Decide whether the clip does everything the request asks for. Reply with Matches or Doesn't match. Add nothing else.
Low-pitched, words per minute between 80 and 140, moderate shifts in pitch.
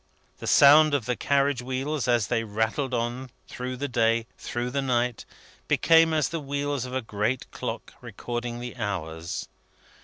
Doesn't match